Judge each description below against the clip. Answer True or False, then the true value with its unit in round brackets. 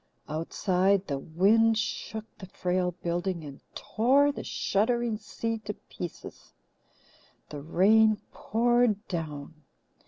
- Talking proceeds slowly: True (105 wpm)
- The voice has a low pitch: False (195 Hz)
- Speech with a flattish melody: False (4.6 semitones)